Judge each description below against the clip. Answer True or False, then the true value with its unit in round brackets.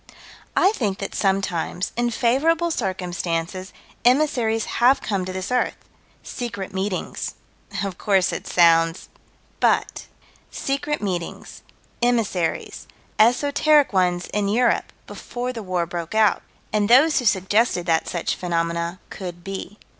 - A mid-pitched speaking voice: False (200 Hz)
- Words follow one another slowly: True (125 wpm)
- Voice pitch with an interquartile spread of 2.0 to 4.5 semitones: False (5.2 semitones)